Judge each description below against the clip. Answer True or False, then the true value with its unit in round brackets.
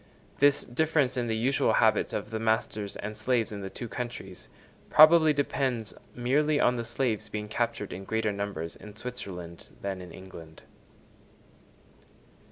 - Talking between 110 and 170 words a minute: True (150 wpm)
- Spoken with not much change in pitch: False (3.9 semitones)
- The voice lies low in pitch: True (110 Hz)